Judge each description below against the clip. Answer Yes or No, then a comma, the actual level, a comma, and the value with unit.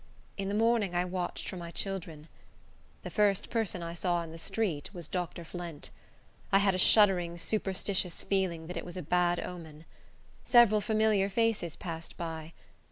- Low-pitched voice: No, medium, 180 Hz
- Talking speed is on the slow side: No, average, 165 wpm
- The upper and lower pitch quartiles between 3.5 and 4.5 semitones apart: No, average, 2.9 semitones